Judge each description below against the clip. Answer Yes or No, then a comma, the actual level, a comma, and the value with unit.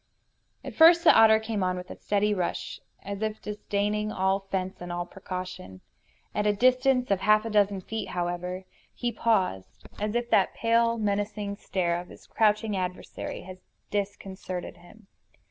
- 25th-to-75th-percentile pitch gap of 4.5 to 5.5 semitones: No, average, 2.9 semitones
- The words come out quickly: No, average, 165 wpm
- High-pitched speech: Yes, high, 200 Hz